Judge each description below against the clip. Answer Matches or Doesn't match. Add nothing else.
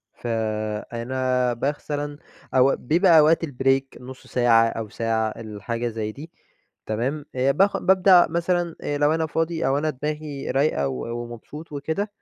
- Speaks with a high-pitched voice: Doesn't match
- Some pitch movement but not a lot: Matches